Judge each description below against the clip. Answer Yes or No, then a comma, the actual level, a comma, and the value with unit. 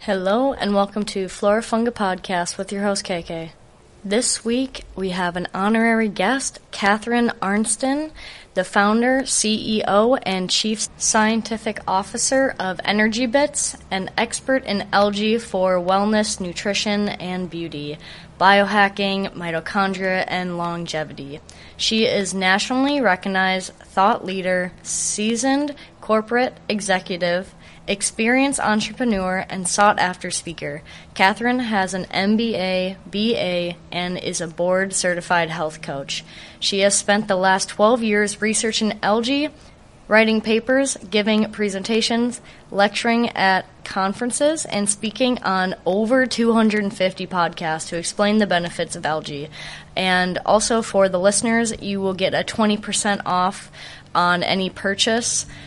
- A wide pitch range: No, average, 3.2 semitones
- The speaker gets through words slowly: Yes, slow, 120 wpm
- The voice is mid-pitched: No, high, 200 Hz